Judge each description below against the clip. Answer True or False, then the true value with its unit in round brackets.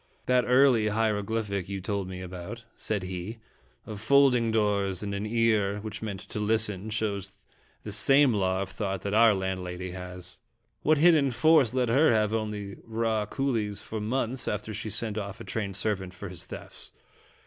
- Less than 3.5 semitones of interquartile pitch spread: True (2.7 semitones)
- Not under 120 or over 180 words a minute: True (175 wpm)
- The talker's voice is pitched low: True (105 Hz)